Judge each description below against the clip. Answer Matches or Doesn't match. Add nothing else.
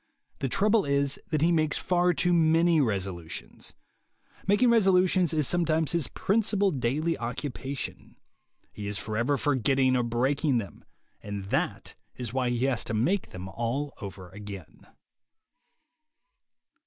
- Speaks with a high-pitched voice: Doesn't match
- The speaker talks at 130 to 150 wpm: Matches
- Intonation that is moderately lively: Doesn't match